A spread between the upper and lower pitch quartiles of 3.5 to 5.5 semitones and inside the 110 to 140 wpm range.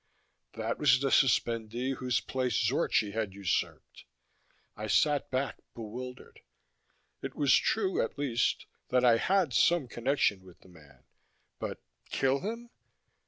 Yes: average, 4.0 semitones; slow, 135 wpm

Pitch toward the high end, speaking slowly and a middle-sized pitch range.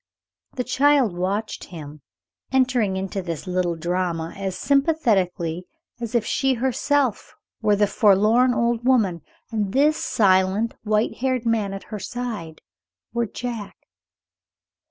Yes: high, 215 Hz; slow, 125 wpm; average, 4.9 semitones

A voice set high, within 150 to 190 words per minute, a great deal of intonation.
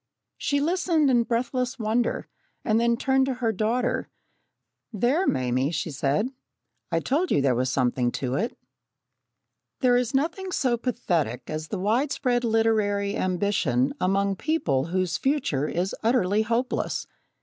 No: high, 220 Hz; average, 140 wpm; wide, 7.3 semitones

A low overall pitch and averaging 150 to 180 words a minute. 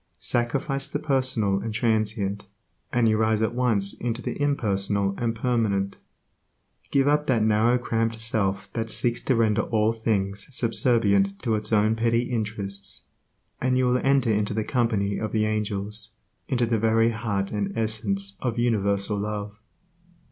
Yes: low, 110 Hz; average, 155 wpm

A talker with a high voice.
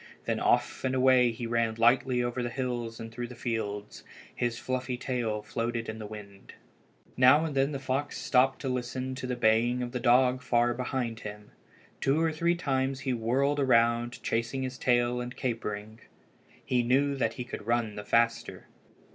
No: low, 120 Hz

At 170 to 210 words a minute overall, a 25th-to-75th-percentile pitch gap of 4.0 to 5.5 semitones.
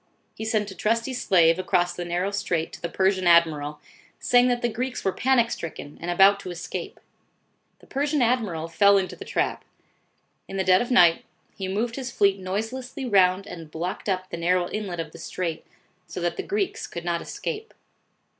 Yes: average, 190 wpm; average, 4.9 semitones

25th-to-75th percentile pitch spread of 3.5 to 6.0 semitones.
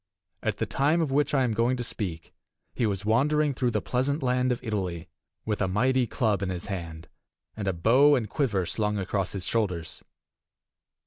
Yes: average, 5.2 semitones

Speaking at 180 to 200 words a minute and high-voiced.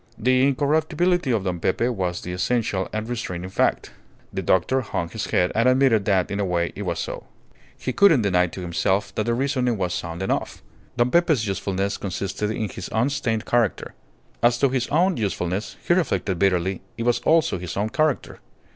No: average, 185 wpm; low, 110 Hz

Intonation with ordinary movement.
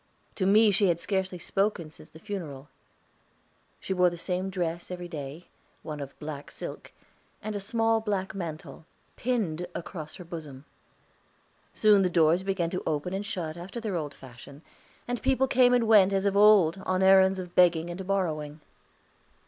Yes: average, 3.7 semitones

